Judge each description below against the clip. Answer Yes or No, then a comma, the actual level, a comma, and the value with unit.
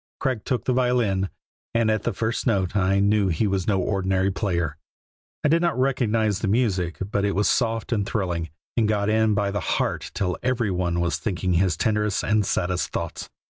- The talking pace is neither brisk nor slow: Yes, average, 195 wpm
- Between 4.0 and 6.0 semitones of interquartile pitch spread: No, average, 3.2 semitones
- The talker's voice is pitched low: Yes, low, 100 Hz